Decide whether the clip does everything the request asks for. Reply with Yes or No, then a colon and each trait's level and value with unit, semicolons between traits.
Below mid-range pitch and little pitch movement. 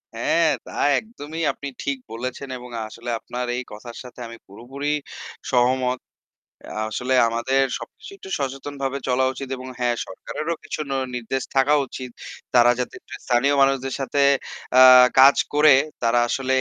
Yes: low, 130 Hz; narrow, 2.2 semitones